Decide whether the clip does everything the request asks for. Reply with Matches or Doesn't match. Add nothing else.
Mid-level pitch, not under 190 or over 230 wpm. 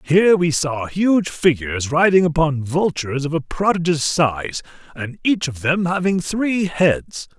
Doesn't match